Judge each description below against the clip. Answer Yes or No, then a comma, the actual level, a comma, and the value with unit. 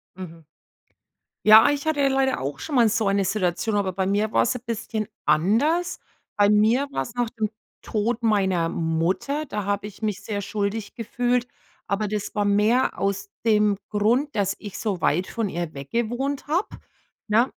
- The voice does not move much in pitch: No, average, 3.5 semitones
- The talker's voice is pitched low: No, high, 215 Hz